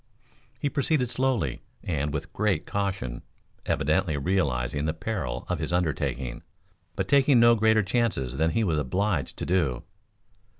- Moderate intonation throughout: No, wide, 7.5 semitones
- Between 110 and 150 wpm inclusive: Yes, average, 140 wpm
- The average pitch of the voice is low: Yes, very low, 90 Hz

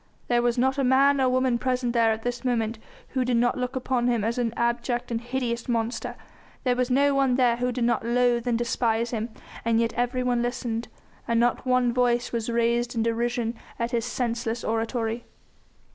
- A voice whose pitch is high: Yes, high, 240 Hz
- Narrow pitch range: Yes, narrow, 1.2 semitones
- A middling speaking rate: Yes, average, 195 wpm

